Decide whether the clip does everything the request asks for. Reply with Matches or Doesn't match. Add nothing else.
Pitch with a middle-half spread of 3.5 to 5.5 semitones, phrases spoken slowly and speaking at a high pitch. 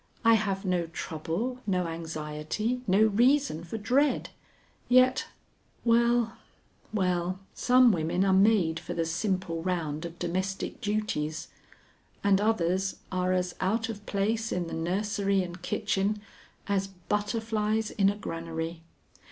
Matches